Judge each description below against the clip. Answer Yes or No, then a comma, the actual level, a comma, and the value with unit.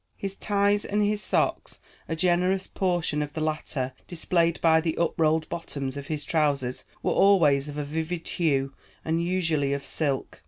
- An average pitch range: Yes, average, 3.6 semitones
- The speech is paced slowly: No, average, 170 wpm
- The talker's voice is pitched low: No, medium, 160 Hz